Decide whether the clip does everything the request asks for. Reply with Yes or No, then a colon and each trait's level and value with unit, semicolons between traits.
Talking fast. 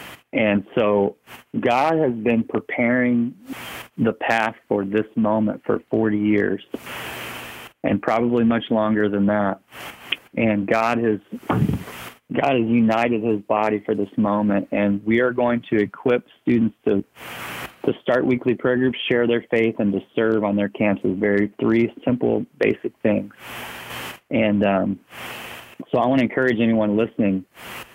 No: average, 145 wpm